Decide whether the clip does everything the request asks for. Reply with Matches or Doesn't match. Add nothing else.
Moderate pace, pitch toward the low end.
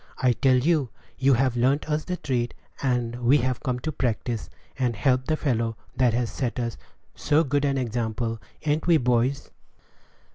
Matches